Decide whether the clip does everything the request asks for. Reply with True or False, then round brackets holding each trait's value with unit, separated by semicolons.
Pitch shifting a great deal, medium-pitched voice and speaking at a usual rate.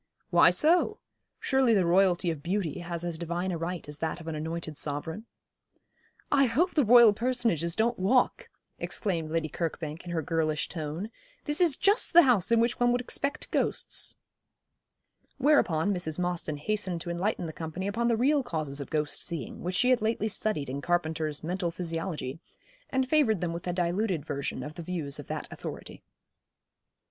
True (6.2 semitones; 175 Hz; 175 wpm)